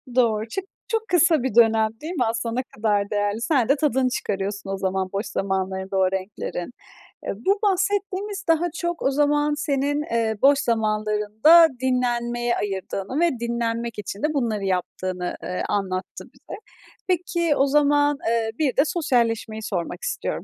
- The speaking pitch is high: Yes, high, 235 Hz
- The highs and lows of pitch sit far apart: Yes, wide, 6.2 semitones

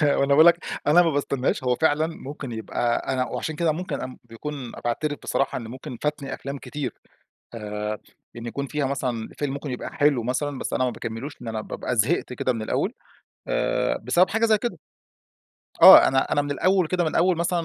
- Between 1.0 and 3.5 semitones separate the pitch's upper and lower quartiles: No, average, 4.0 semitones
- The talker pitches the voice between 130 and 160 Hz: Yes, medium, 140 Hz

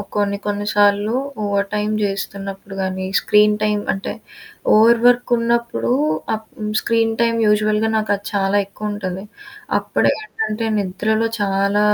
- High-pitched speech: Yes, high, 210 Hz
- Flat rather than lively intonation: Yes, narrow, 1.7 semitones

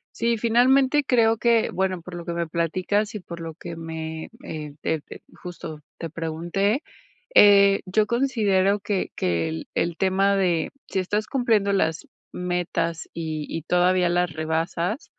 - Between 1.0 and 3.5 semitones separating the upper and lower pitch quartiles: No, average, 4.0 semitones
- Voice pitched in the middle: Yes, medium, 180 Hz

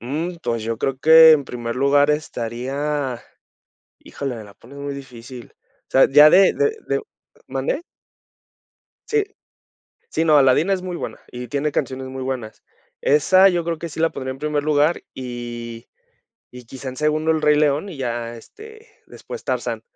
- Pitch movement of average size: Yes, average, 4.2 semitones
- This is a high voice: No, medium, 140 Hz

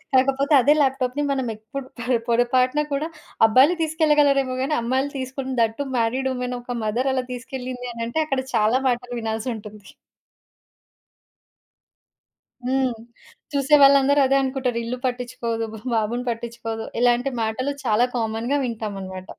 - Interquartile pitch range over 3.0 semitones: No, average, 2.7 semitones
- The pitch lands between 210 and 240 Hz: No, very high, 250 Hz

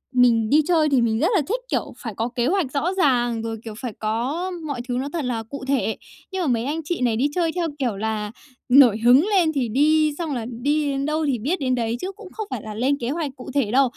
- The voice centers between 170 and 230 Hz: No, very high, 270 Hz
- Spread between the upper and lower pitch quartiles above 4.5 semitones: Yes, average, 4.9 semitones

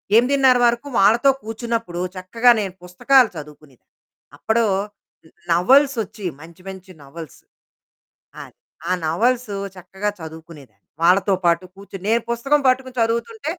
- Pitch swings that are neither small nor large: No, wide, 5.8 semitones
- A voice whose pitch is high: Yes, high, 205 Hz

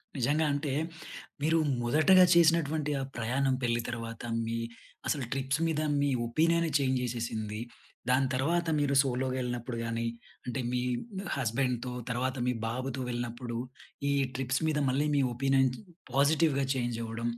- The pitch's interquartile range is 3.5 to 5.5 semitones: No, average, 3.1 semitones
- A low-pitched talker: Yes, low, 130 Hz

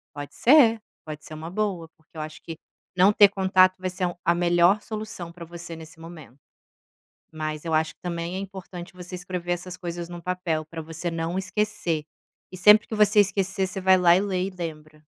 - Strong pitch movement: No, narrow, 2.6 semitones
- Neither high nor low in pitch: Yes, medium, 175 Hz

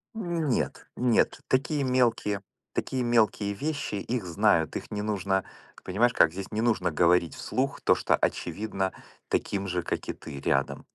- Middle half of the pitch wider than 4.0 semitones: Yes, average, 4.9 semitones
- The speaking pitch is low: Yes, low, 105 Hz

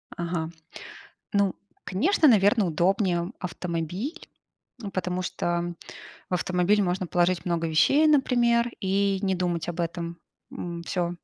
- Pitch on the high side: No, medium, 180 Hz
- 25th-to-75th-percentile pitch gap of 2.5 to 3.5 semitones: Yes, average, 2.8 semitones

